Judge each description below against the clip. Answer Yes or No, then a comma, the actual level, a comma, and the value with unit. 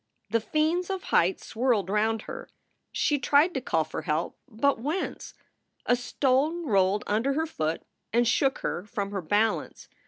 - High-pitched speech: Yes, high, 240 Hz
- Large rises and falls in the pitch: Yes, wide, 6.1 semitones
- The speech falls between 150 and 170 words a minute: Yes, average, 160 wpm